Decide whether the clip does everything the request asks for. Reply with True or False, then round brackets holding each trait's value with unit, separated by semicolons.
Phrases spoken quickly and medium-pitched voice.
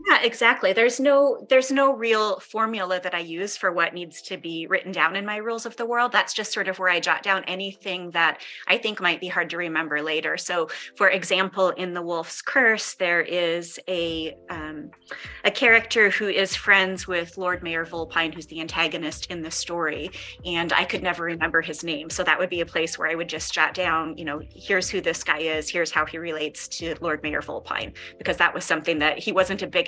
True (225 wpm; 175 Hz)